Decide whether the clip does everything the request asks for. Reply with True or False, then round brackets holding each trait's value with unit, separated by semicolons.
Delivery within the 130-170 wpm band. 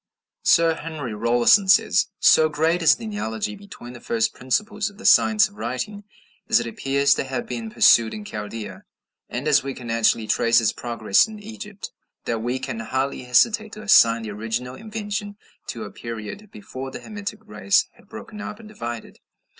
False (180 wpm)